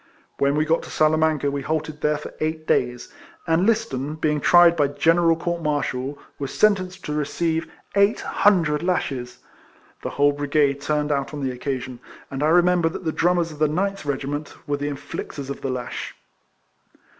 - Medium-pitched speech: Yes, medium, 150 Hz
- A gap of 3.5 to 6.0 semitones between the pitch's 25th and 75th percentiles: No, average, 2.8 semitones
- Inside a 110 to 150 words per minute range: No, average, 180 wpm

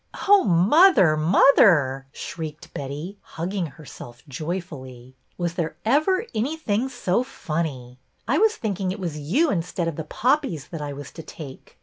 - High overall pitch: No, medium, 170 Hz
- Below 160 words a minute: No, average, 165 wpm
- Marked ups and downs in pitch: Yes, wide, 6.9 semitones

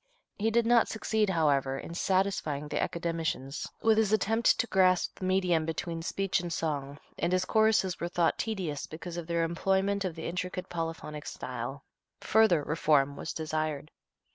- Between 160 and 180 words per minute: Yes, average, 165 wpm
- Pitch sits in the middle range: Yes, medium, 170 Hz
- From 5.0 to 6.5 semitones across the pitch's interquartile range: No, average, 3.8 semitones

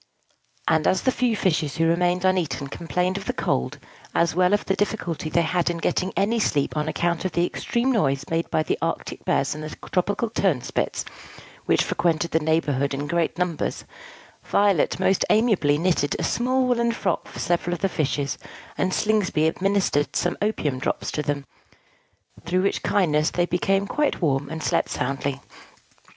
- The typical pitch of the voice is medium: Yes, medium, 175 Hz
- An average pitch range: Yes, average, 4.2 semitones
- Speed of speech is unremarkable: Yes, average, 175 wpm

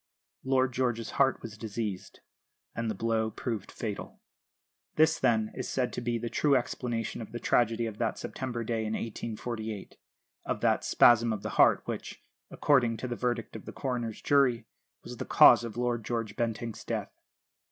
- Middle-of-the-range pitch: No, low, 115 Hz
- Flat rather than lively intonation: Yes, narrow, 1.8 semitones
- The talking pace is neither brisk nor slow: Yes, average, 175 wpm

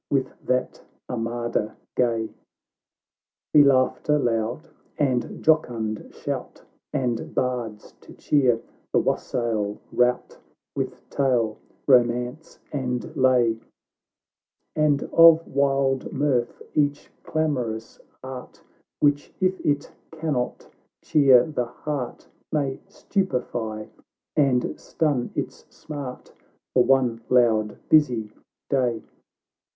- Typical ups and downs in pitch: Yes, average, 3.4 semitones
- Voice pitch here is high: No, low, 125 Hz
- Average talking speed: No, slow, 95 wpm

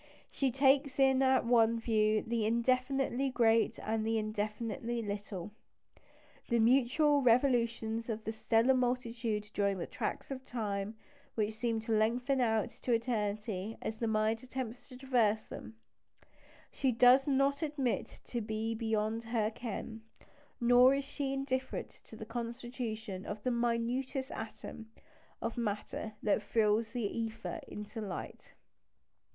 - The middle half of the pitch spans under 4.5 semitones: Yes, average, 2.7 semitones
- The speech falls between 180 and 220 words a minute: No, slow, 135 wpm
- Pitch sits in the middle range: No, high, 230 Hz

